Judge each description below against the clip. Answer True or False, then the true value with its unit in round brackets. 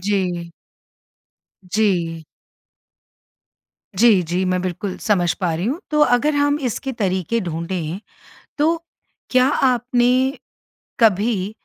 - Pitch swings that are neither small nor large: False (5.8 semitones)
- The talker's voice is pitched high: True (205 Hz)